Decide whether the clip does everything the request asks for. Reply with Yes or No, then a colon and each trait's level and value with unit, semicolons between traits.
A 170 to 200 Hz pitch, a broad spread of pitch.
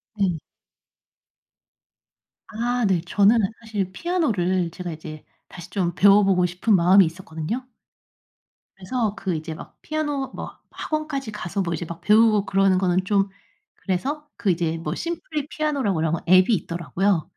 No: high, 195 Hz; average, 4.8 semitones